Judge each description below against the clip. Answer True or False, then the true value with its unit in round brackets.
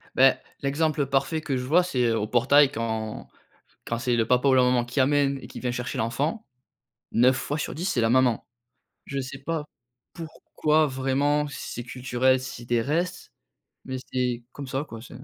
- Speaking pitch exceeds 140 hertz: False (130 Hz)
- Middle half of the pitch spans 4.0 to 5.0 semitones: False (2.9 semitones)